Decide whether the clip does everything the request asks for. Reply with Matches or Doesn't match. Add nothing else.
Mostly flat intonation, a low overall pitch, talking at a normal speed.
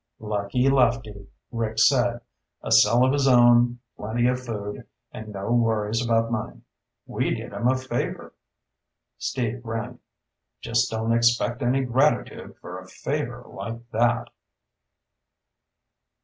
Doesn't match